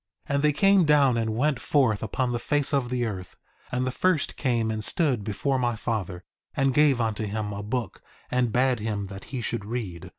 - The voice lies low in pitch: Yes, low, 120 Hz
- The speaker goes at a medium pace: No, fast, 210 wpm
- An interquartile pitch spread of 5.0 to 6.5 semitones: No, average, 4.0 semitones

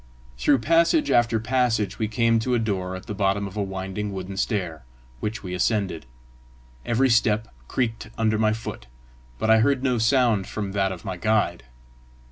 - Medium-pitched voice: No, low, 110 Hz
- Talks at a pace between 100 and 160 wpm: No, average, 175 wpm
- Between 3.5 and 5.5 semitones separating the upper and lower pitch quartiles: No, average, 3.1 semitones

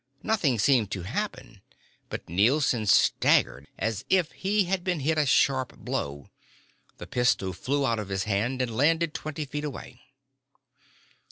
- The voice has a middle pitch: No, low, 130 Hz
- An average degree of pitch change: No, wide, 6.3 semitones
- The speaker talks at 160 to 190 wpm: No, average, 150 wpm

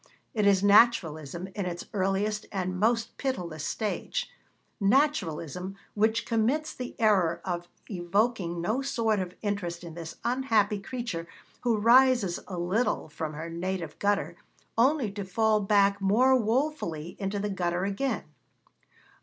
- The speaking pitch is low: No, high, 200 Hz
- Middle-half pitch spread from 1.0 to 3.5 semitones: No, average, 4.5 semitones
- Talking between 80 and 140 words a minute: Yes, slow, 135 wpm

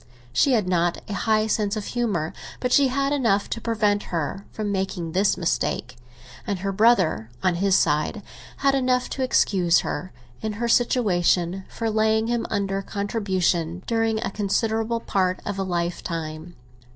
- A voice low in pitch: No, high, 200 Hz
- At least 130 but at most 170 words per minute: Yes, average, 160 wpm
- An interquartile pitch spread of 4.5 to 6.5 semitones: No, average, 3.8 semitones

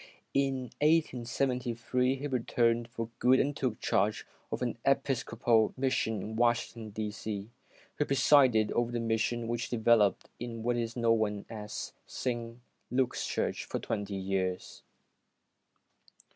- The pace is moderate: No, slow, 130 wpm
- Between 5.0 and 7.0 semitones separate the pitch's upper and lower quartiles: No, narrow, 2.4 semitones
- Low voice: Yes, low, 120 Hz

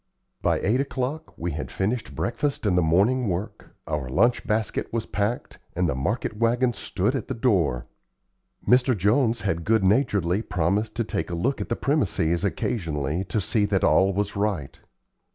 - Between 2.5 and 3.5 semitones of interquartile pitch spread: No, average, 5.2 semitones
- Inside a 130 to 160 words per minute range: No, average, 170 wpm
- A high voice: No, low, 105 Hz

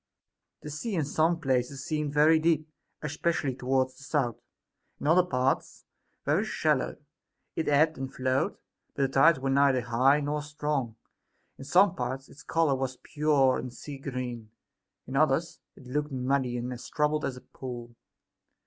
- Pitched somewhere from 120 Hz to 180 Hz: Yes, medium, 140 Hz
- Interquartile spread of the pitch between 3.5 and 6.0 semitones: No, average, 2.8 semitones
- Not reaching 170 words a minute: Yes, average, 160 wpm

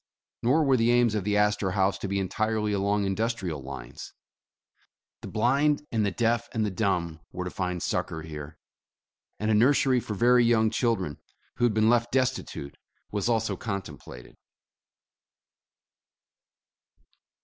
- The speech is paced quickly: No, average, 150 wpm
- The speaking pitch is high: No, low, 105 Hz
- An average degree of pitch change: Yes, average, 3.9 semitones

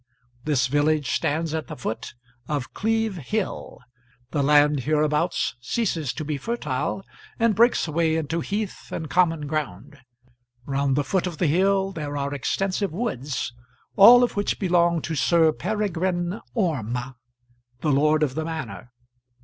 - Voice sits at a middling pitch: Yes, medium, 160 Hz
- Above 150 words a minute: No, average, 145 wpm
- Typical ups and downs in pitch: Yes, average, 4.6 semitones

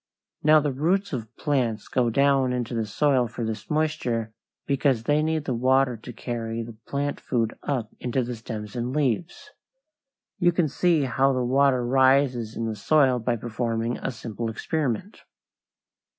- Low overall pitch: Yes, low, 125 Hz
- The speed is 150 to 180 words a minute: Yes, average, 165 wpm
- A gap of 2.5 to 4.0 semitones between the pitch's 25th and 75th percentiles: Yes, average, 3.7 semitones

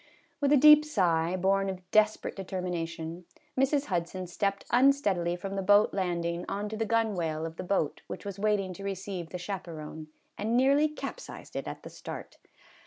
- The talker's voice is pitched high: Yes, high, 195 Hz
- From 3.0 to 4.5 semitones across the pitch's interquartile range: Yes, average, 3.7 semitones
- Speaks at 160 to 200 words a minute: Yes, average, 175 wpm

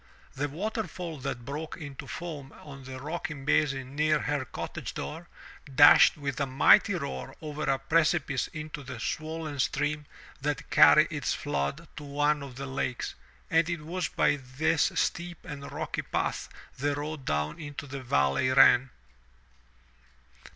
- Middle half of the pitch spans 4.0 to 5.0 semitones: No, average, 2.7 semitones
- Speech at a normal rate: Yes, average, 150 wpm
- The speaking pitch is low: No, medium, 145 Hz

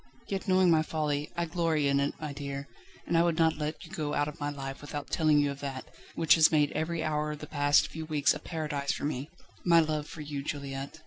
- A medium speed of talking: No, fast, 245 wpm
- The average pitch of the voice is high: No, medium, 150 Hz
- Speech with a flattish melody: Yes, narrow, 1.9 semitones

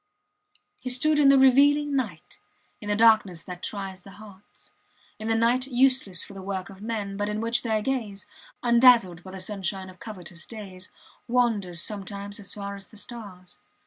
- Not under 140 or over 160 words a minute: No, average, 175 wpm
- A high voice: Yes, high, 210 Hz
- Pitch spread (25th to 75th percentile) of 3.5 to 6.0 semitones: Yes, average, 3.8 semitones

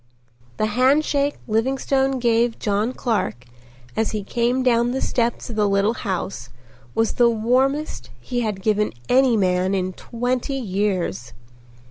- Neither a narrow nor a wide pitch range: Yes, average, 3.9 semitones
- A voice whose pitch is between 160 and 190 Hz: No, high, 230 Hz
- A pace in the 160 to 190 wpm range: No, slow, 135 wpm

